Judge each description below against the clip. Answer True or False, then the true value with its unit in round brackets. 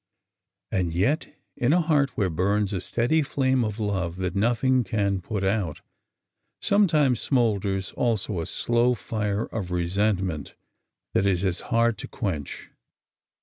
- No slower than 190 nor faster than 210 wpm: False (145 wpm)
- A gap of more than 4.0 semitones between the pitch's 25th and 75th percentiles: True (4.4 semitones)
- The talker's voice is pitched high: False (105 Hz)